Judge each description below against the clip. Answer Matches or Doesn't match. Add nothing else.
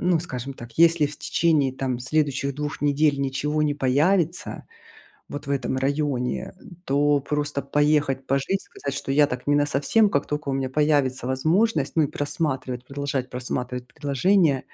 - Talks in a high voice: Doesn't match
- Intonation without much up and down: Matches